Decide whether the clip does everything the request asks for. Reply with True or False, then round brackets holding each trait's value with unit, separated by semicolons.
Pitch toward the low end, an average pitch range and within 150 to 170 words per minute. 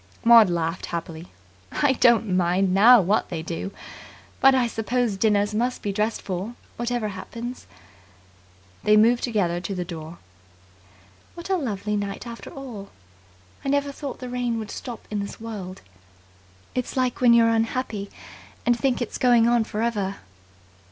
False (225 Hz; 3.7 semitones; 155 wpm)